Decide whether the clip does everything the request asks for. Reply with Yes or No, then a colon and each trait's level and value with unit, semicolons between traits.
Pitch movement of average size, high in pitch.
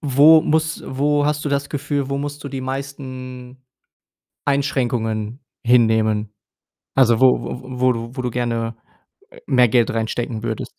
No: average, 3.3 semitones; low, 130 Hz